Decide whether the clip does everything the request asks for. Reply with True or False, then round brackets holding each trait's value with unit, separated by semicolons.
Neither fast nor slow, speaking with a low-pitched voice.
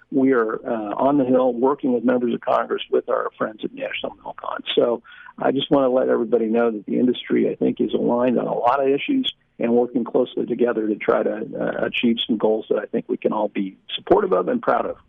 False (245 wpm; 130 Hz)